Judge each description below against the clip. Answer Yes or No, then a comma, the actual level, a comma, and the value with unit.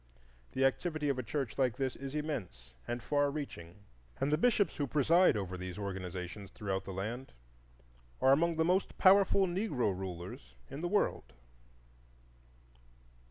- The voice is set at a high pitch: No, low, 135 Hz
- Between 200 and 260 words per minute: No, average, 150 wpm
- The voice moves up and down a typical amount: No, wide, 8.2 semitones